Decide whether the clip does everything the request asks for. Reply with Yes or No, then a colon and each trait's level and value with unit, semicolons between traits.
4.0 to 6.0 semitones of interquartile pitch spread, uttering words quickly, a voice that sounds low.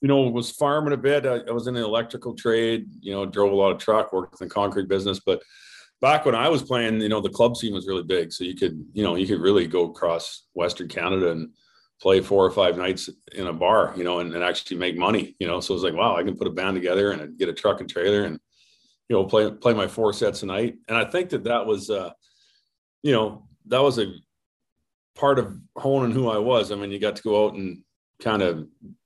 Yes: average, 5.3 semitones; fast, 255 wpm; low, 110 Hz